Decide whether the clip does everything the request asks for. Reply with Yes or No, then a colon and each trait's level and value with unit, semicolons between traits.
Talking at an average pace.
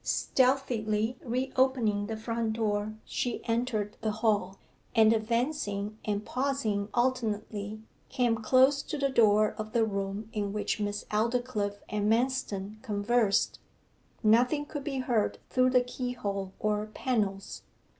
No: slow, 130 wpm